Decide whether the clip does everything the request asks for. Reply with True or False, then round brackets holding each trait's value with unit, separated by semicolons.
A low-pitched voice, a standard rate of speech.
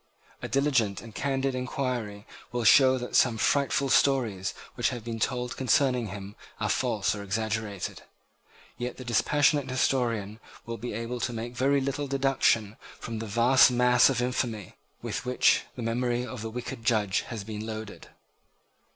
True (120 Hz; 160 wpm)